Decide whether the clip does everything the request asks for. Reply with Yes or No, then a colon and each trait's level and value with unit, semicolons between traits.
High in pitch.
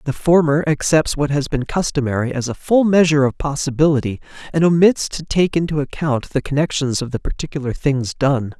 No: medium, 145 Hz